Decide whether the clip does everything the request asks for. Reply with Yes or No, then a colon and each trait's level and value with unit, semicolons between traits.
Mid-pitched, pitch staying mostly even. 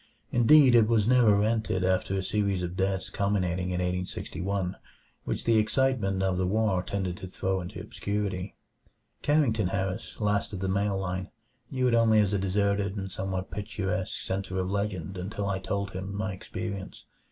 No: low, 100 Hz; narrow, 2.1 semitones